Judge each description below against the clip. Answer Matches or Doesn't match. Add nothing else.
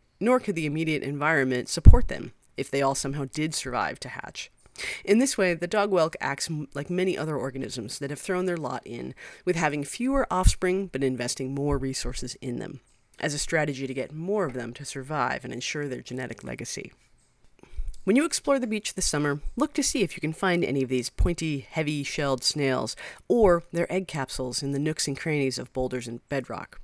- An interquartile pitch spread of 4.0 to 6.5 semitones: Matches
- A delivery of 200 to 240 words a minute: Matches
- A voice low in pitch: Doesn't match